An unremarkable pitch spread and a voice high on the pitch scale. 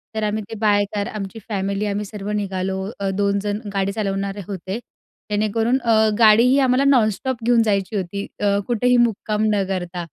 No: narrow, 2.1 semitones; high, 205 Hz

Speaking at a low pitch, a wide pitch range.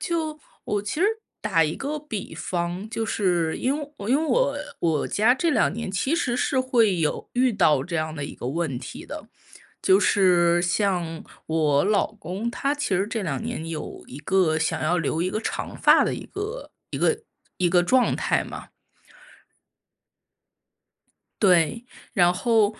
No: high, 190 Hz; wide, 6.5 semitones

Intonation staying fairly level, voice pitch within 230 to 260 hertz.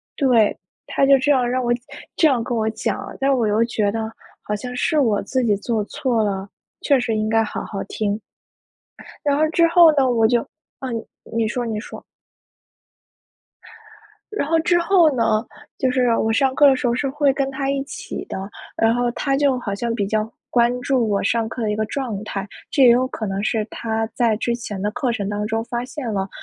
No: average, 3.7 semitones; high, 240 Hz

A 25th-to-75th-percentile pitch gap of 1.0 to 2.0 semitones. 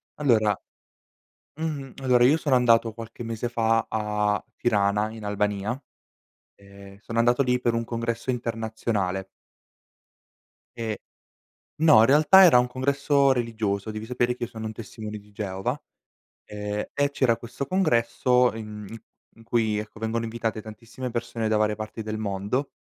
No: narrow, 2.5 semitones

